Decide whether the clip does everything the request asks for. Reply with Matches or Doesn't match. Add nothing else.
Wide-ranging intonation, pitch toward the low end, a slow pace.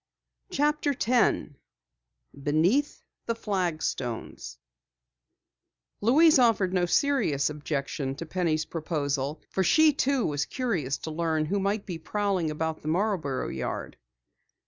Doesn't match